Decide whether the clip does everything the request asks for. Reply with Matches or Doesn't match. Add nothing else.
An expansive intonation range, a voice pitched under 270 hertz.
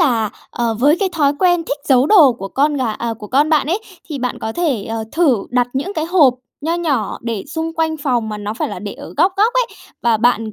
Doesn't match